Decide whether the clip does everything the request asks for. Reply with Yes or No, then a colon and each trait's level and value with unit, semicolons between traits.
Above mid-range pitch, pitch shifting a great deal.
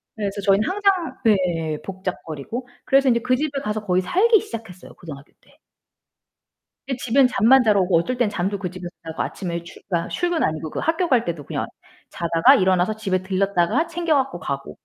Yes: high, 205 Hz; wide, 6.8 semitones